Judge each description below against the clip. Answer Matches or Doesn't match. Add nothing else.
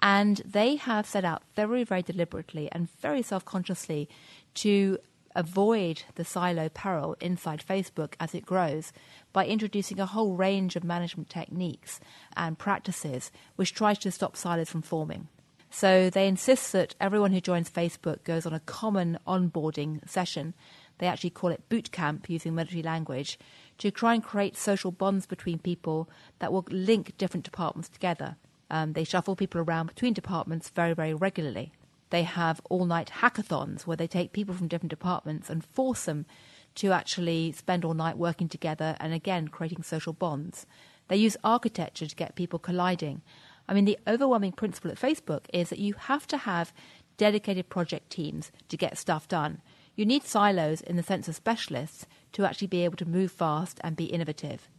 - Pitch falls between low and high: Matches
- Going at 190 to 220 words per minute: Doesn't match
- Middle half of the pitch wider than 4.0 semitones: Doesn't match